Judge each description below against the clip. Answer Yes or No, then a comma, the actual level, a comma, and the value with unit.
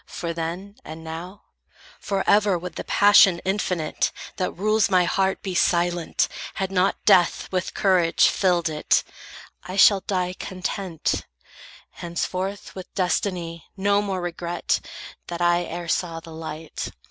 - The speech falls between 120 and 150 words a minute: Yes, slow, 135 wpm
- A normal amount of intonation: No, narrow, 2.2 semitones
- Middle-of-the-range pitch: Yes, medium, 180 Hz